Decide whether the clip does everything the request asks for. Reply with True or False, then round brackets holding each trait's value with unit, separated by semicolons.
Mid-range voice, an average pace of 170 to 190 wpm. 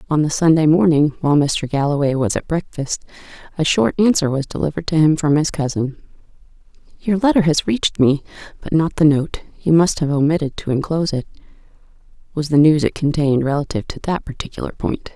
True (155 Hz; 180 wpm)